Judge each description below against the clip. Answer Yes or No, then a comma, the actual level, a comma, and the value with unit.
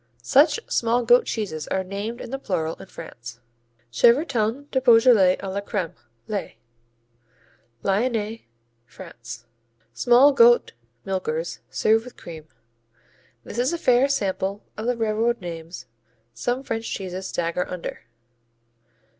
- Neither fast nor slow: No, slow, 125 wpm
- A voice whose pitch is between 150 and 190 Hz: No, high, 215 Hz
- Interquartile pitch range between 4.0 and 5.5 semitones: Yes, average, 5.1 semitones